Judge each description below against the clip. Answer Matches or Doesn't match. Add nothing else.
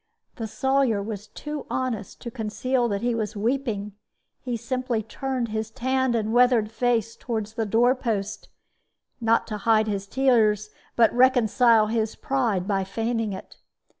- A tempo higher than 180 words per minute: Doesn't match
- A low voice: Doesn't match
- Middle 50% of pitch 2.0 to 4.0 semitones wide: Matches